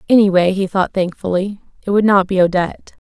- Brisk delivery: No, average, 175 wpm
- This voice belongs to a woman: Yes, female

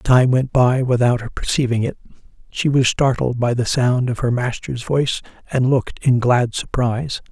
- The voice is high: No, low, 125 Hz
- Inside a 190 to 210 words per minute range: No, average, 180 wpm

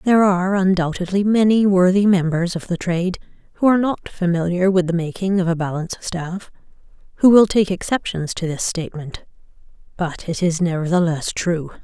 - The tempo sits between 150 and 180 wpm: Yes, average, 160 wpm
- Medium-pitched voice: Yes, medium, 180 Hz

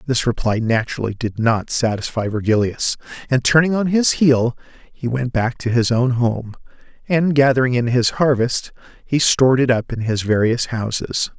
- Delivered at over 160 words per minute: Yes, average, 170 wpm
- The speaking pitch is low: Yes, low, 125 Hz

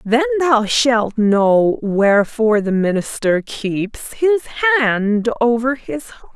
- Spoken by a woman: Yes, female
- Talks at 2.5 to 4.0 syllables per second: Yes, 3.4 syllables/s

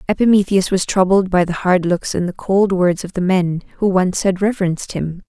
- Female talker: Yes, female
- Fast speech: Yes, fast, 215 wpm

